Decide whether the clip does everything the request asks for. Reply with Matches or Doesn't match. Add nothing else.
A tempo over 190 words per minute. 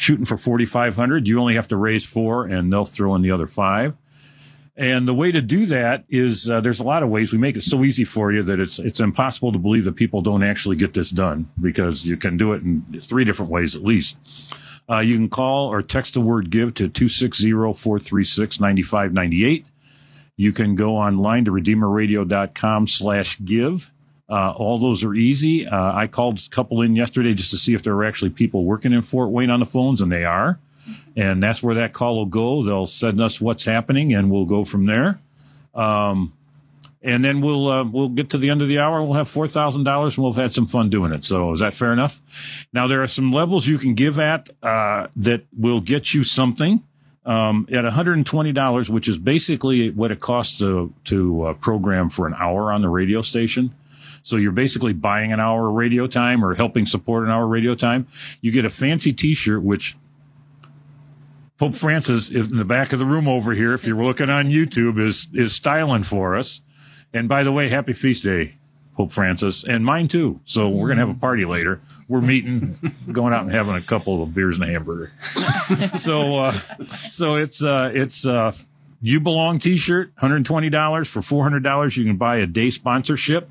Matches